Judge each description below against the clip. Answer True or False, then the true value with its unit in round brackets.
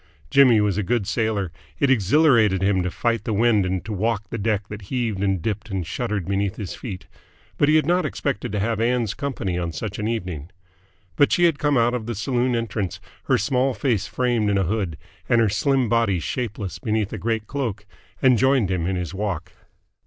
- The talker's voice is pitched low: True (110 Hz)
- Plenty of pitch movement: False (3.9 semitones)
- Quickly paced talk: True (210 wpm)